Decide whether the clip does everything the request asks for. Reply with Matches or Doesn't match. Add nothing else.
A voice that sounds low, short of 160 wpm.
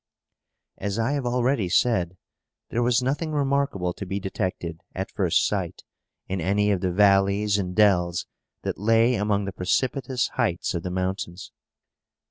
Matches